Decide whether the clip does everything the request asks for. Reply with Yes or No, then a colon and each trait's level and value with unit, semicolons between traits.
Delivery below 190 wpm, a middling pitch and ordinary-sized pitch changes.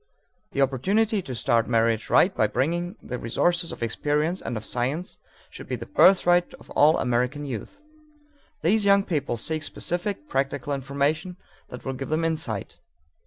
No: average, 160 wpm; medium, 145 Hz; wide, 5.9 semitones